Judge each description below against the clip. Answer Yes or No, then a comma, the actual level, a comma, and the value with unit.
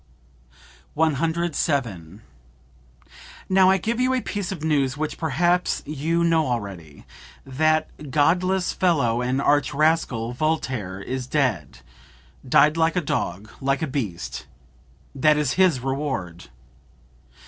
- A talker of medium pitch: Yes, medium, 145 Hz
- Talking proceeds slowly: Yes, slow, 115 wpm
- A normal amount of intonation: No, wide, 6.0 semitones